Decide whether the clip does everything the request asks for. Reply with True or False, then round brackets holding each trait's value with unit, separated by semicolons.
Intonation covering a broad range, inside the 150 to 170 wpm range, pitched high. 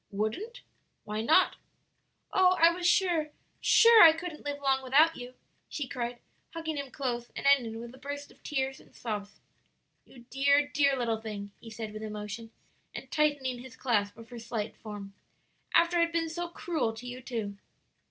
False (5.7 semitones; 180 wpm; 260 Hz)